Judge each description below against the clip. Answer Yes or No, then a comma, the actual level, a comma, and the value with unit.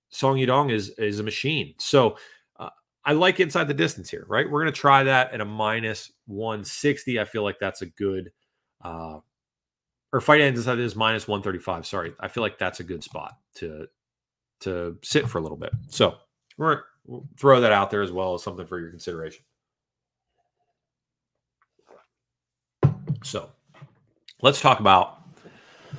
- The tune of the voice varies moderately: No, wide, 6.5 semitones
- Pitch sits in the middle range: No, low, 110 Hz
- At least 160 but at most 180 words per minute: Yes, average, 165 wpm